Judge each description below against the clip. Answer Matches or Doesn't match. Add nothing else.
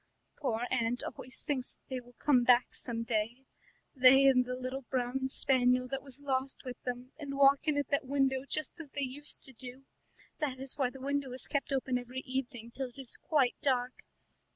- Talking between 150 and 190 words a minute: Doesn't match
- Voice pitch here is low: Doesn't match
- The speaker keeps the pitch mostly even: Matches